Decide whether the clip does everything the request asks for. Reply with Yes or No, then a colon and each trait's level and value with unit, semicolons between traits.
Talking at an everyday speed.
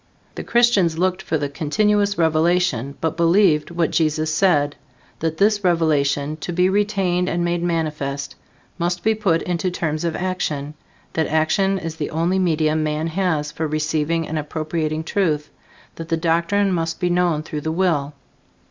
Yes: average, 160 wpm